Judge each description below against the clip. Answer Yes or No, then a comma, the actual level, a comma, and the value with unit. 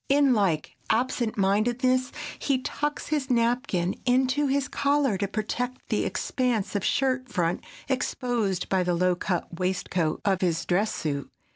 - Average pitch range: No, wide, 5.9 semitones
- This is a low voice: No, high, 230 Hz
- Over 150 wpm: No, average, 145 wpm